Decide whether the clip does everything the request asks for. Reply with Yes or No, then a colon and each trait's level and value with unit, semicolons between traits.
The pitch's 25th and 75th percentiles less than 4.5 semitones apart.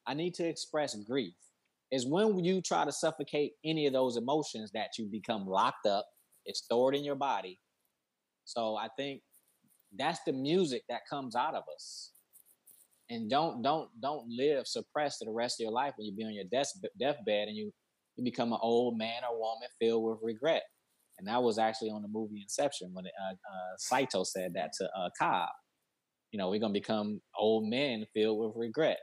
No: average, 5.1 semitones